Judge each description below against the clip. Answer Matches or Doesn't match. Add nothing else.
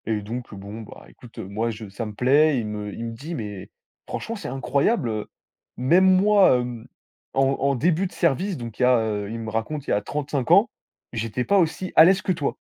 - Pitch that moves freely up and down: Matches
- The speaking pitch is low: Matches